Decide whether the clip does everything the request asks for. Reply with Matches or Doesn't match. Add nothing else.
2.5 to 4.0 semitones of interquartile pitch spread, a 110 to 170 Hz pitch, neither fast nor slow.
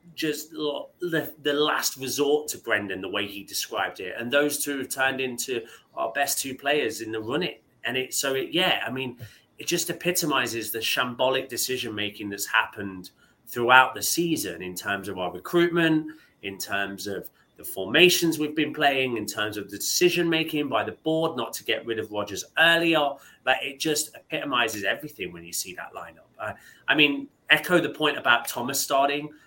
Doesn't match